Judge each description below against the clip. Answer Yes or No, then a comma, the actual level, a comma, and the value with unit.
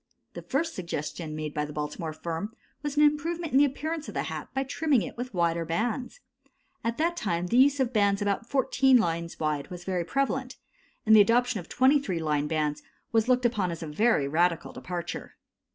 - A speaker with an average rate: Yes, average, 195 wpm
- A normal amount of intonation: No, wide, 8.0 semitones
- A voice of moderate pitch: No, high, 210 Hz